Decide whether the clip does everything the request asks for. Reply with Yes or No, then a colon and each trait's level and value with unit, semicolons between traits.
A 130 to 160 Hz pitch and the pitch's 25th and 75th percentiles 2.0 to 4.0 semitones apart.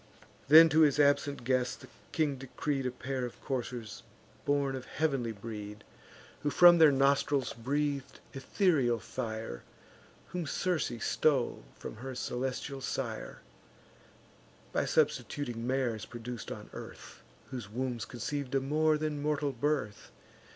Yes: low, 135 Hz; average, 3.4 semitones